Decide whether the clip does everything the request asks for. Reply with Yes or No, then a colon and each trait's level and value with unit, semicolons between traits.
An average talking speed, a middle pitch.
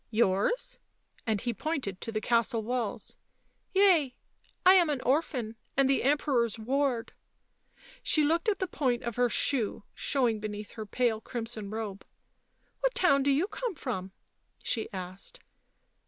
No: average, 160 wpm; high, 245 Hz